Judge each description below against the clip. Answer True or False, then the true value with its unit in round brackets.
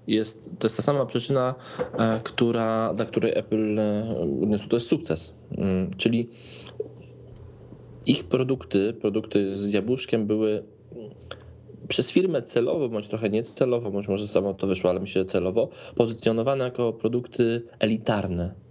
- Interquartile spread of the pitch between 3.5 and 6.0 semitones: False (2.6 semitones)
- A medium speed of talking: True (120 wpm)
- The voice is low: True (110 Hz)